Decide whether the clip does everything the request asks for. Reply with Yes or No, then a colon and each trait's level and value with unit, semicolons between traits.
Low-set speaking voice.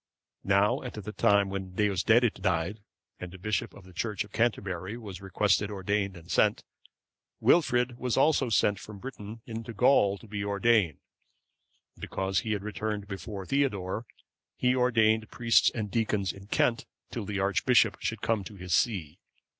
Yes: low, 105 Hz